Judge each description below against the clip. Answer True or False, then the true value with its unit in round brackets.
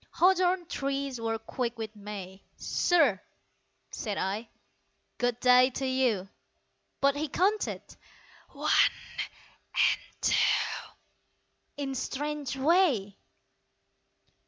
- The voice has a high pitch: True (260 Hz)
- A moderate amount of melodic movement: True (4.9 semitones)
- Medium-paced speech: False (90 wpm)